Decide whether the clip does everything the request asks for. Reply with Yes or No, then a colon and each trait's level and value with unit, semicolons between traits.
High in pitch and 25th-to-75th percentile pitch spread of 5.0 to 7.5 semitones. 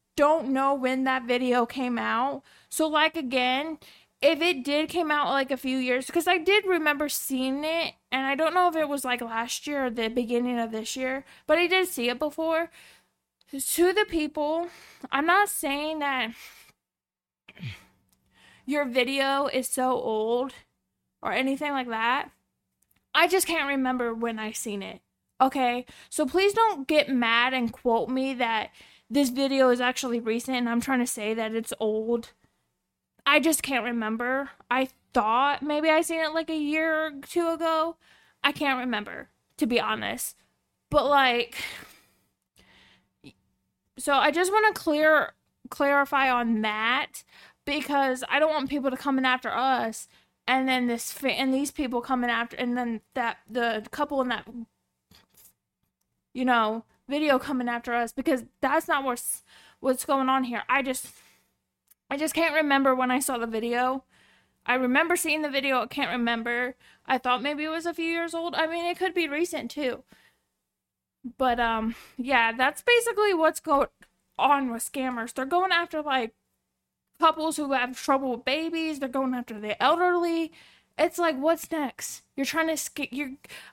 No: very high, 270 Hz; average, 3.9 semitones